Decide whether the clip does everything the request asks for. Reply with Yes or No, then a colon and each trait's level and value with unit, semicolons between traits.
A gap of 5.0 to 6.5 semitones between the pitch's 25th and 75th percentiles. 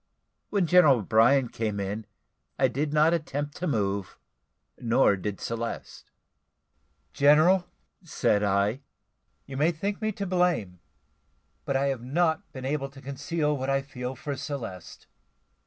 Yes: average, 5.3 semitones